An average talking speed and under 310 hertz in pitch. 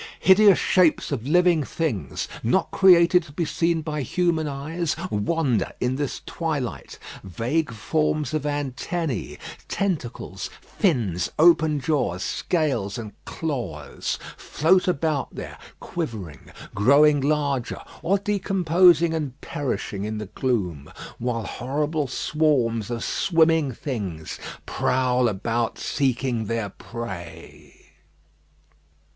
No: slow, 105 wpm; medium, 140 Hz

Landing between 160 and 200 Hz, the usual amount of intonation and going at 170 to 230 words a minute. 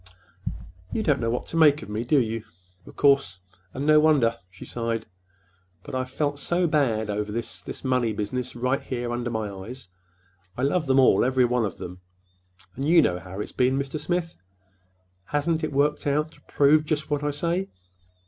No: low, 130 Hz; average, 4.4 semitones; average, 180 wpm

